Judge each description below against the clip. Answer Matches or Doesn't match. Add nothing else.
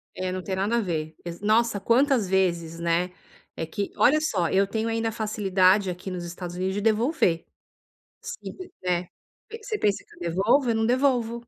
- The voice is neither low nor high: Doesn't match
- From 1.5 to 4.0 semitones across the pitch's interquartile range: Doesn't match